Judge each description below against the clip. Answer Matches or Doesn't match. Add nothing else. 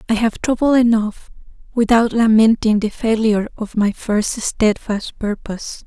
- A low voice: Doesn't match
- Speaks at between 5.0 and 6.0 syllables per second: Doesn't match